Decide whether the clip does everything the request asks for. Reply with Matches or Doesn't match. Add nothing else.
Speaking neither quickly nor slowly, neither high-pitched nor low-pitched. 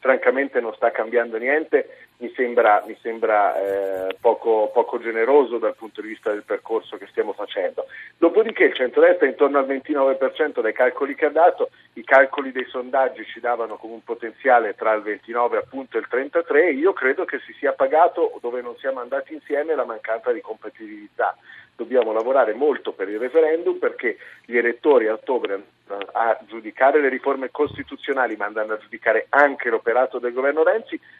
Doesn't match